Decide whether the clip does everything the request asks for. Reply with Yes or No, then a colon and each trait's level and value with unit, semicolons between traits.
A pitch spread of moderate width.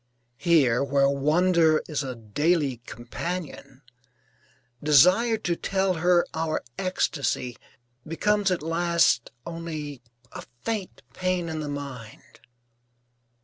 Yes: average, 4.3 semitones